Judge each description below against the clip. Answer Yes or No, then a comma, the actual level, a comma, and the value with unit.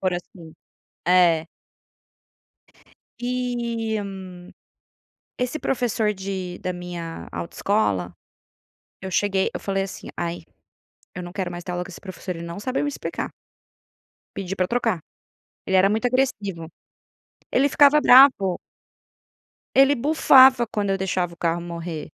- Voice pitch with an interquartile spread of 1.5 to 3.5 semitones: No, wide, 5.4 semitones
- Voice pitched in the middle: No, high, 195 Hz